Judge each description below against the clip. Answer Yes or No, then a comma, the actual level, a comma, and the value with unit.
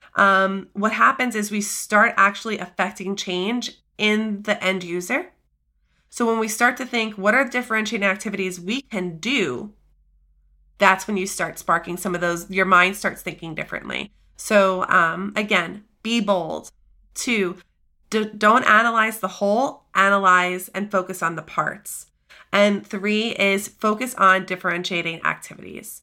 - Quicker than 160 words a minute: No, average, 145 wpm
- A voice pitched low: No, high, 195 Hz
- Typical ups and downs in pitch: Yes, average, 3.0 semitones